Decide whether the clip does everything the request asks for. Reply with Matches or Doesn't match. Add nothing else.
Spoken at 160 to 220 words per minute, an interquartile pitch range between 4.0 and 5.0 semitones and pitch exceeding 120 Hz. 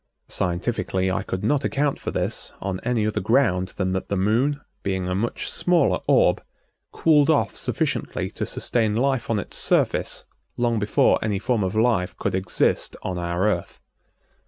Doesn't match